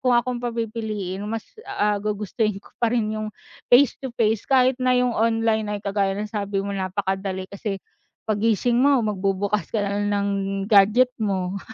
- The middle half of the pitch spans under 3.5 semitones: Yes, average, 2.7 semitones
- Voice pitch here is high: Yes, high, 210 Hz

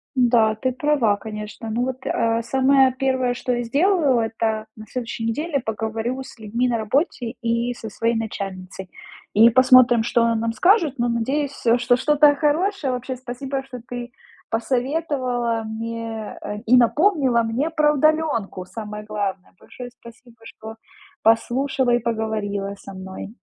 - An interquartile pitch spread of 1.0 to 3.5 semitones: Yes, average, 3.0 semitones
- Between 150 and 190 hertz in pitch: No, high, 240 Hz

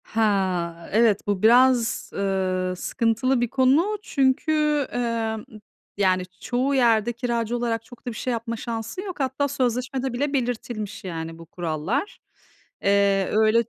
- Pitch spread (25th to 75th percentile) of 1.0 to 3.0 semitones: No, average, 4.1 semitones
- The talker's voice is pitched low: No, high, 235 Hz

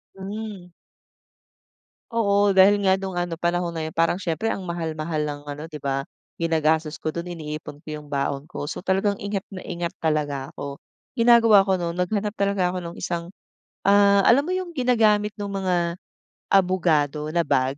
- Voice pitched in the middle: Yes, medium, 175 Hz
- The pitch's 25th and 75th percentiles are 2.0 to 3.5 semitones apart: No, average, 4.3 semitones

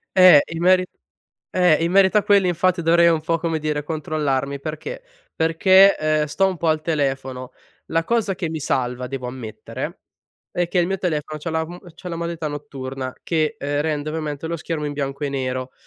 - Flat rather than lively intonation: No, average, 3.1 semitones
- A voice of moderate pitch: Yes, medium, 155 Hz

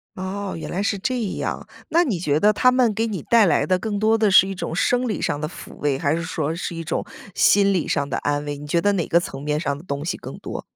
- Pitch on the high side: No, medium, 180 Hz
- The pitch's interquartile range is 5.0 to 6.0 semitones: Yes, wide, 5.6 semitones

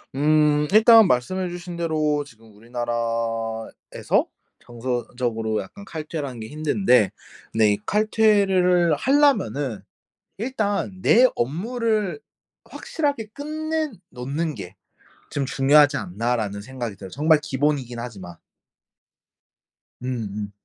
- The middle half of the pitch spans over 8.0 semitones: Yes, wide, 8.6 semitones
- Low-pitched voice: No, medium, 145 Hz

